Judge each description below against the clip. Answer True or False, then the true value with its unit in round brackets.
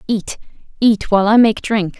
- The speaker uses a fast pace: False (180 wpm)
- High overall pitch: True (215 Hz)